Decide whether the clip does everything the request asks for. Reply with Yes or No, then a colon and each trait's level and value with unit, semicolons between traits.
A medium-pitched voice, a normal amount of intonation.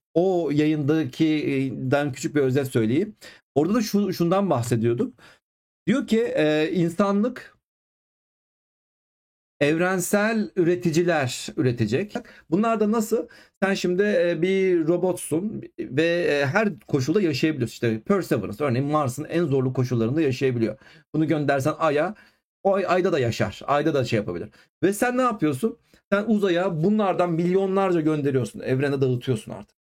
No: medium, 165 Hz; wide, 5.7 semitones